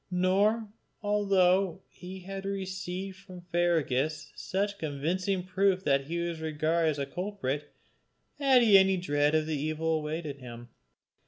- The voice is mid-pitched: Yes, medium, 175 Hz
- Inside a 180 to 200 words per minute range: No, slow, 135 wpm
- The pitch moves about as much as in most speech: Yes, average, 3.9 semitones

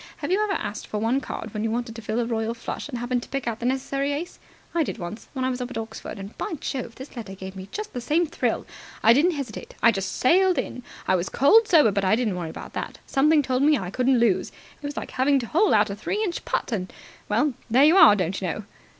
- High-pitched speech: Yes, high, 245 Hz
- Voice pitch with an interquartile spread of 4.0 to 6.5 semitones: Yes, average, 5.1 semitones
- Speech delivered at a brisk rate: Yes, fast, 270 wpm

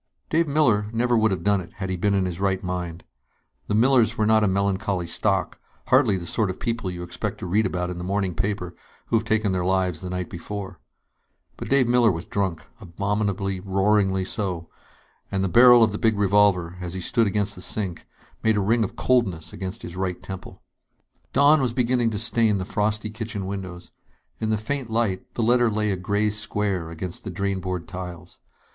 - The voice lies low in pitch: Yes, low, 100 Hz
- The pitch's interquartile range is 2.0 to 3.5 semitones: Yes, average, 3.1 semitones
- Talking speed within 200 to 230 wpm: Yes, fast, 205 wpm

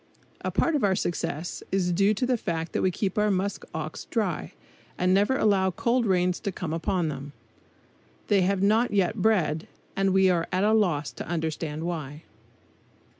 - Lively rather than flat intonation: No, average, 3.6 semitones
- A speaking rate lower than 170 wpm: No, average, 180 wpm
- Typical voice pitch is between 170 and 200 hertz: Yes, medium, 185 Hz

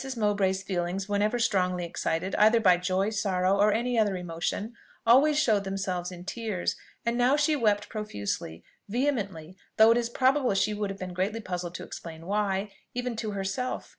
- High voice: Yes, high, 200 Hz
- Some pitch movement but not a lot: Yes, average, 3.7 semitones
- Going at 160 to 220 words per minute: Yes, average, 170 wpm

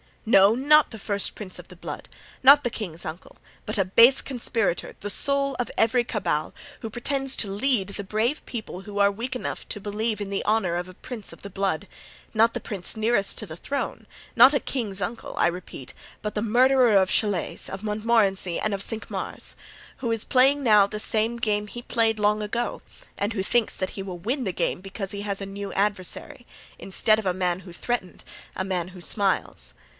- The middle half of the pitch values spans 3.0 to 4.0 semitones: Yes, average, 3.4 semitones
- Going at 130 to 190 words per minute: No, average, 200 wpm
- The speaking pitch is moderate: No, high, 210 Hz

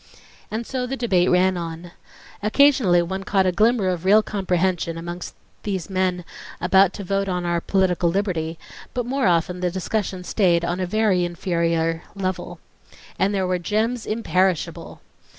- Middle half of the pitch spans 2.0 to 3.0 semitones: Yes, average, 2.7 semitones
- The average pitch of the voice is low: No, medium, 185 Hz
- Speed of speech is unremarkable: Yes, average, 155 wpm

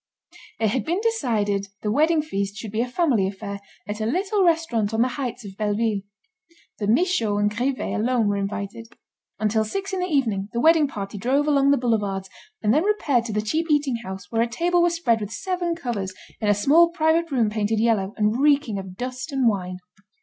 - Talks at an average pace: No, fast, 210 wpm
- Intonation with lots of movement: Yes, wide, 6.4 semitones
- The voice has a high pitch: Yes, high, 230 Hz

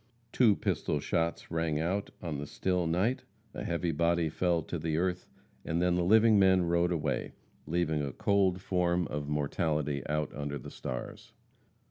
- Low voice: Yes, very low, 85 Hz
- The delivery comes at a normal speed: Yes, average, 165 wpm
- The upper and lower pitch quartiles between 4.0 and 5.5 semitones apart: No, average, 2.9 semitones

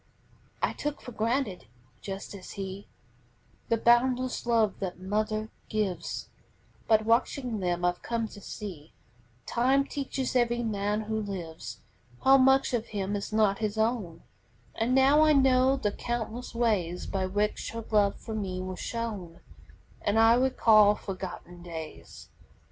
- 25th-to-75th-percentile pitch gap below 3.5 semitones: No, average, 3.8 semitones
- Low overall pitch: No, high, 215 Hz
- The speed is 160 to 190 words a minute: No, average, 145 wpm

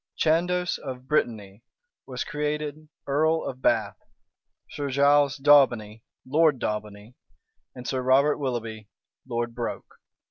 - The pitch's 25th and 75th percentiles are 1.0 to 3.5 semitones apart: No, average, 4.0 semitones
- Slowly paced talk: Yes, slow, 110 wpm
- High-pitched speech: No, low, 135 Hz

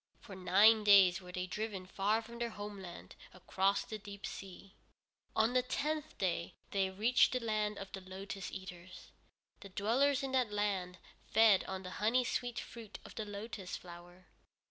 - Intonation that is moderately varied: Yes, average, 3.1 semitones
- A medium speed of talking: Yes, average, 165 wpm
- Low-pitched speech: No, high, 200 Hz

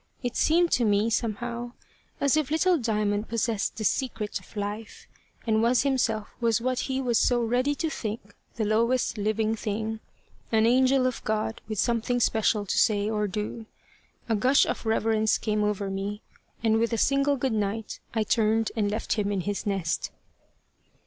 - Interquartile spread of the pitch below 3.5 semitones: Yes, narrow, 2.6 semitones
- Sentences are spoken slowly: No, average, 170 wpm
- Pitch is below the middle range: No, high, 225 Hz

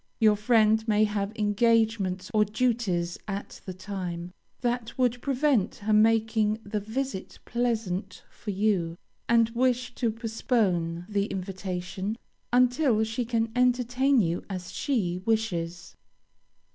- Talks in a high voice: Yes, high, 215 Hz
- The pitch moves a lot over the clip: No, average, 3.8 semitones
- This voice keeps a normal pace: No, slow, 120 wpm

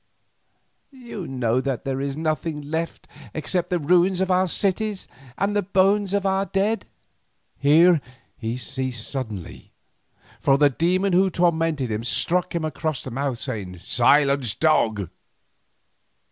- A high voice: No, medium, 155 Hz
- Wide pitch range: Yes, wide, 6.0 semitones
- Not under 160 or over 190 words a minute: No, slow, 135 wpm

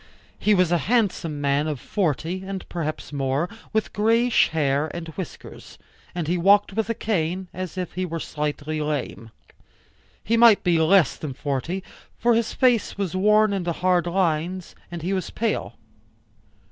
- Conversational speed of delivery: Yes, average, 160 wpm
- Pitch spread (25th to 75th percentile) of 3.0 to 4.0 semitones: No, average, 4.4 semitones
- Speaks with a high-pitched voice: No, medium, 180 Hz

